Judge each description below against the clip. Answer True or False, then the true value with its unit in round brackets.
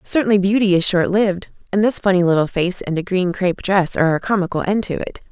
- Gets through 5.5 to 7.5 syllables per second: True (6.3 syllables/s)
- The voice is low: False (190 Hz)